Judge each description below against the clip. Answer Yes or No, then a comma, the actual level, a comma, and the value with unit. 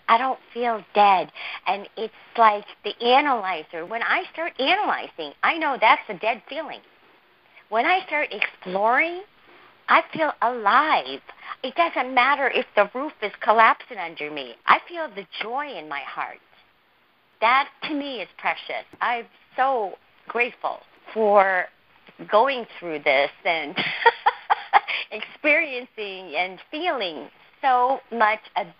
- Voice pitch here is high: Yes, high, 240 Hz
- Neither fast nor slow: No, slow, 125 wpm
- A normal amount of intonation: No, wide, 6.2 semitones